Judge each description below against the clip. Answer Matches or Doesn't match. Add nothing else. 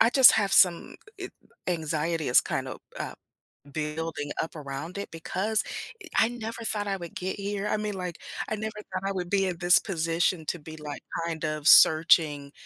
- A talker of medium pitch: Matches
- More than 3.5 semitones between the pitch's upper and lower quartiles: Matches